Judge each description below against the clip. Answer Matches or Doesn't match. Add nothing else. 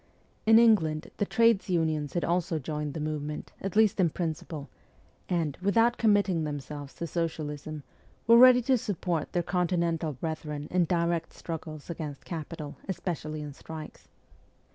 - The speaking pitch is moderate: Matches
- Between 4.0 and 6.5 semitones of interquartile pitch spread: Doesn't match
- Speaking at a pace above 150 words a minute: Doesn't match